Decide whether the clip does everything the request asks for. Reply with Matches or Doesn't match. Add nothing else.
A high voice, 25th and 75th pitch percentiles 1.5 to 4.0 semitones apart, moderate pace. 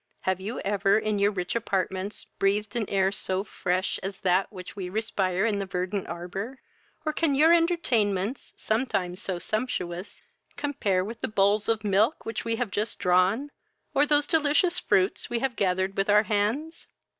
Matches